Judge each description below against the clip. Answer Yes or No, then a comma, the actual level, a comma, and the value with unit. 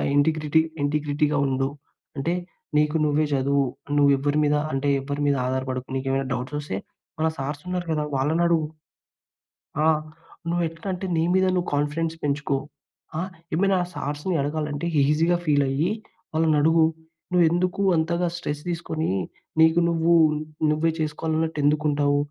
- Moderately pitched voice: Yes, medium, 150 Hz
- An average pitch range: No, narrow, 2.3 semitones